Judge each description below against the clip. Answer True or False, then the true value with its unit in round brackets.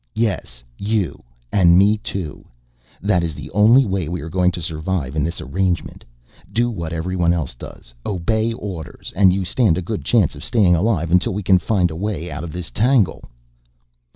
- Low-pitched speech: True (90 Hz)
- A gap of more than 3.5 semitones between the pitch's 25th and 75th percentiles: True (4.0 semitones)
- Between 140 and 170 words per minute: False (185 wpm)